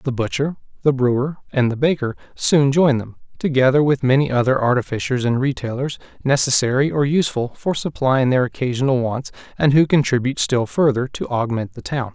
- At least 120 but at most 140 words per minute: No, average, 170 wpm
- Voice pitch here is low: Yes, low, 130 Hz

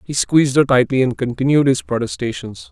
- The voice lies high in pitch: No, low, 130 Hz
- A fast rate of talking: No, average, 175 wpm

